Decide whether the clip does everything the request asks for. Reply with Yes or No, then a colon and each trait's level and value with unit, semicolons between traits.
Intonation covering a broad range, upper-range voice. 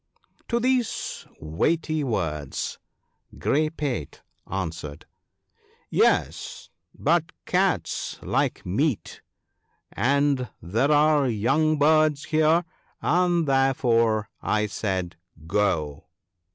No: wide, 7.9 semitones; low, 135 Hz